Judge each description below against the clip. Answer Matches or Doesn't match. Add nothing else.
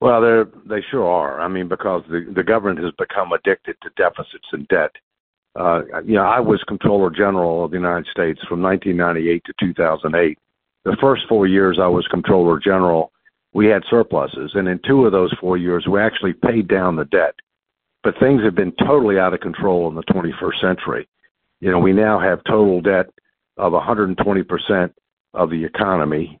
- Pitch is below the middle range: Matches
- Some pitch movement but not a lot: Matches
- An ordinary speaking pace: Matches